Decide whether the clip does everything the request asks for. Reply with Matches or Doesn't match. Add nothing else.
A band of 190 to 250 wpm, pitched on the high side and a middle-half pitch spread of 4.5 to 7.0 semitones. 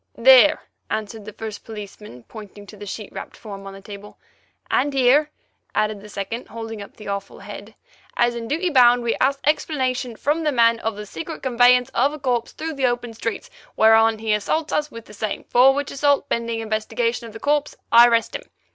Doesn't match